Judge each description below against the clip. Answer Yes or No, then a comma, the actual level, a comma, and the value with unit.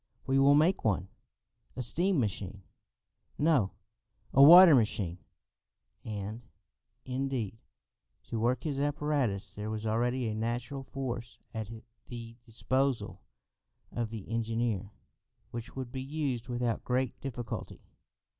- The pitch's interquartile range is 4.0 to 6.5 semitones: No, average, 3.6 semitones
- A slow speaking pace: Yes, slow, 115 wpm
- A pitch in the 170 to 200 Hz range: No, low, 120 Hz